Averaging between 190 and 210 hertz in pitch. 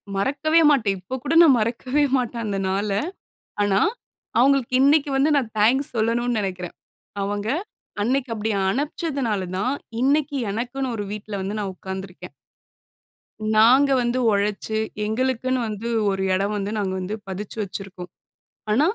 No: high, 225 Hz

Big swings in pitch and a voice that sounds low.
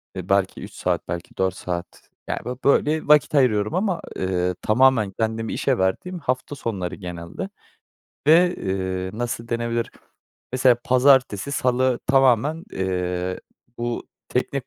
Yes: wide, 6.0 semitones; low, 115 Hz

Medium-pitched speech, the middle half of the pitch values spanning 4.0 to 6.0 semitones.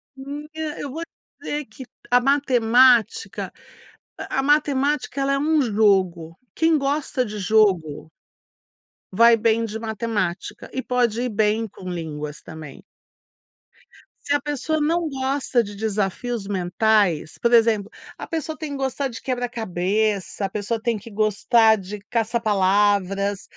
No: high, 225 Hz; average, 5.1 semitones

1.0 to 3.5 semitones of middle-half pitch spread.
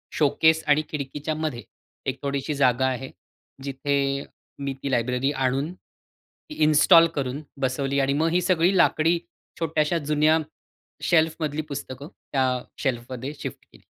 Yes: average, 2.9 semitones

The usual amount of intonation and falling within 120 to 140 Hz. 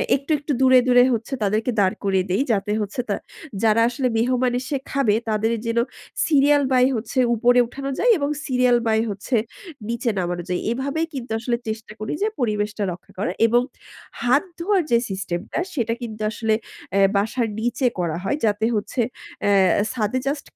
No: average, 3.6 semitones; high, 235 Hz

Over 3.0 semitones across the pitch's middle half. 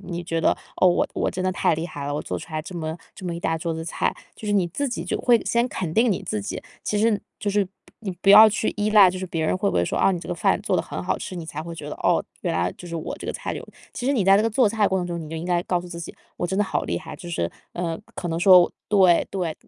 Yes: average, 3.5 semitones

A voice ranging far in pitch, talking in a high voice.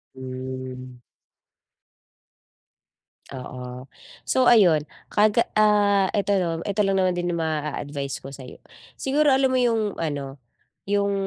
No: wide, 7.7 semitones; medium, 170 Hz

